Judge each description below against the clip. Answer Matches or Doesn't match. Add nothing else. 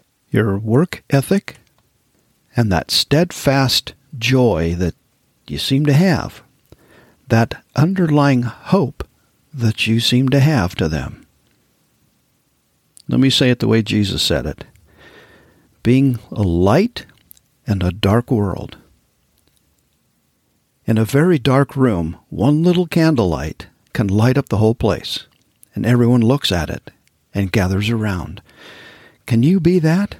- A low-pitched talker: Matches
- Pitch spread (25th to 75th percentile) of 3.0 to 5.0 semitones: Doesn't match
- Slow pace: Matches